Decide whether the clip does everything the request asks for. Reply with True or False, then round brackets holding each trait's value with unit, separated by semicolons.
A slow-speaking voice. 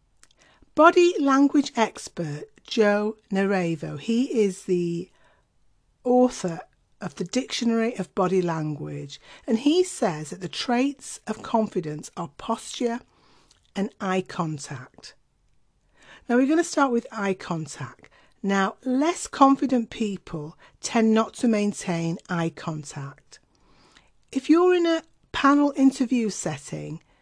True (115 wpm)